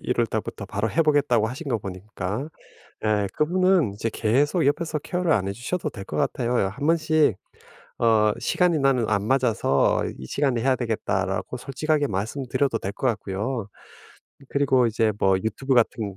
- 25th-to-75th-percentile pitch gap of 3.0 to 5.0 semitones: No, wide, 5.5 semitones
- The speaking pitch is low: Yes, low, 120 Hz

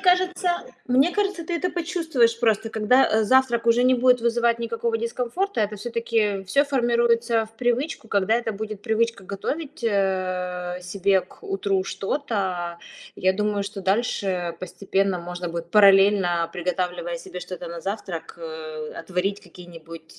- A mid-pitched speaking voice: No, high, 205 Hz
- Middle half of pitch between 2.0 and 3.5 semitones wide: No, average, 4.6 semitones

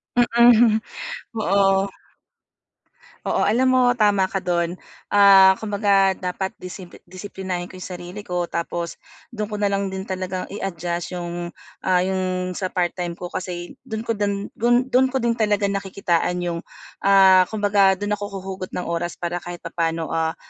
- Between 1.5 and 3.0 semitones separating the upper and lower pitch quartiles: Yes, narrow, 2.5 semitones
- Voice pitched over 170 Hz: Yes, high, 190 Hz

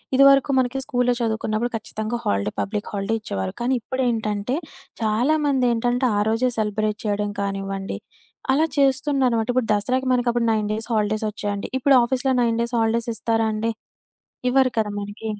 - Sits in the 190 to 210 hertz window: No, high, 225 Hz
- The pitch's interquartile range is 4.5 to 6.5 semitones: No, average, 3.2 semitones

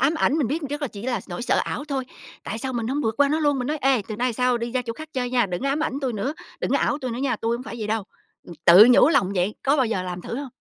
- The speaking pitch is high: Yes, very high, 250 Hz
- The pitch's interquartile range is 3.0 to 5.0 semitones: Yes, average, 3.9 semitones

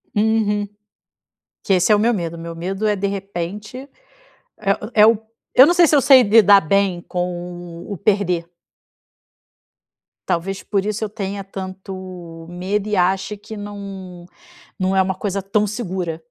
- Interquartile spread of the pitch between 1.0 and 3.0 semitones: Yes, narrow, 2.5 semitones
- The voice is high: Yes, high, 195 Hz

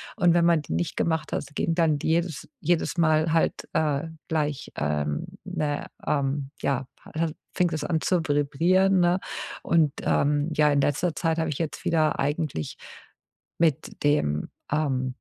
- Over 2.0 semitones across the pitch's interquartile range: Yes, narrow, 2.6 semitones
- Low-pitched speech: No, medium, 155 Hz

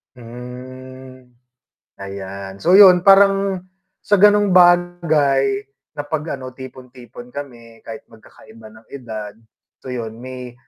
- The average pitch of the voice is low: Yes, low, 130 Hz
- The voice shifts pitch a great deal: Yes, wide, 6.9 semitones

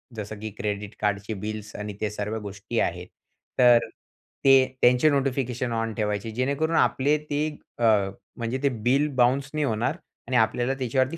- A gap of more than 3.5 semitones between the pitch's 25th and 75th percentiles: Yes, average, 4.0 semitones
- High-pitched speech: No, low, 120 Hz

